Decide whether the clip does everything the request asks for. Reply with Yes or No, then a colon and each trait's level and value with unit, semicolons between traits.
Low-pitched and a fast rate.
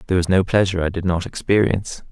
Yes: very low, 95 Hz; fast, 225 wpm